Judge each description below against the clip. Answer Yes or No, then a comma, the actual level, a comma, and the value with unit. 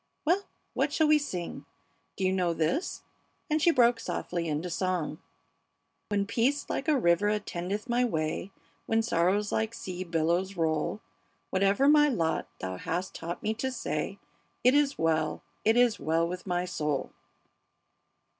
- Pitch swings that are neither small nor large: No, wide, 6.1 semitones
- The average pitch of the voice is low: No, high, 190 Hz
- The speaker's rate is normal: Yes, average, 155 wpm